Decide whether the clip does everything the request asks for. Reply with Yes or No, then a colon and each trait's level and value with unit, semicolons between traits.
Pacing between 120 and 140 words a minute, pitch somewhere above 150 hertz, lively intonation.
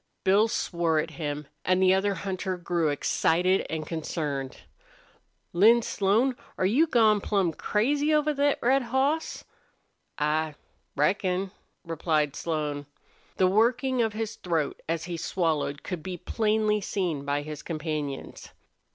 Yes: slow, 135 wpm; medium, 185 Hz; wide, 5.8 semitones